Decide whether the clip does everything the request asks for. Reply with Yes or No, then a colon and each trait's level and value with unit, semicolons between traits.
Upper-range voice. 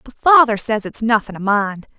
Yes: high, 225 Hz